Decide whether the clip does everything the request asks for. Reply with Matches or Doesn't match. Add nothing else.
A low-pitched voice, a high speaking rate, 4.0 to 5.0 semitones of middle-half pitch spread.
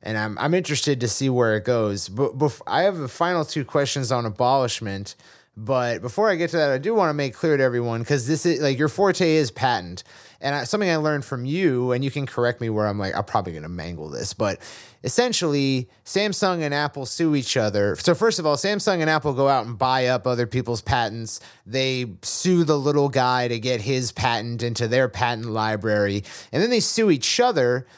Matches